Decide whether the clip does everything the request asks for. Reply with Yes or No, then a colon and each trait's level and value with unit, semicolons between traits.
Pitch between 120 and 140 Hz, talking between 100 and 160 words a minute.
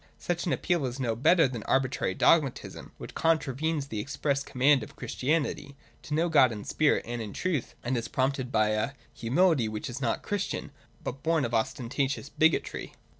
No: low, 135 Hz; average, 180 wpm